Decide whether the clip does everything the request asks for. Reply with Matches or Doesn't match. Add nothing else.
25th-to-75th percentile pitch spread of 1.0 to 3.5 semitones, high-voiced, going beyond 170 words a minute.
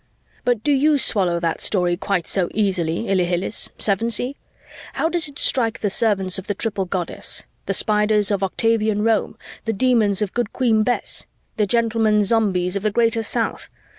Doesn't match